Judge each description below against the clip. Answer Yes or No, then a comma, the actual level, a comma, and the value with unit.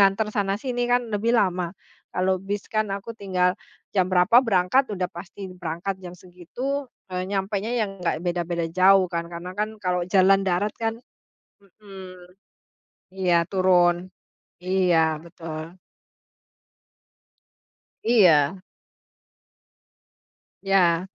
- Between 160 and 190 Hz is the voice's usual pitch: Yes, medium, 185 Hz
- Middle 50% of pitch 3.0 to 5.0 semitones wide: No, narrow, 2.4 semitones